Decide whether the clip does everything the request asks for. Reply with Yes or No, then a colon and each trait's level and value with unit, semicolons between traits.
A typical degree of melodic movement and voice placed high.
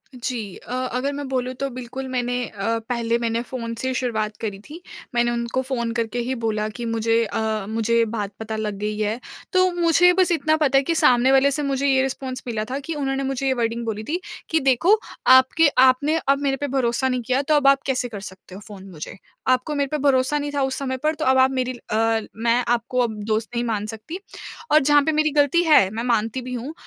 Yes: average, 3.2 semitones; very high, 255 Hz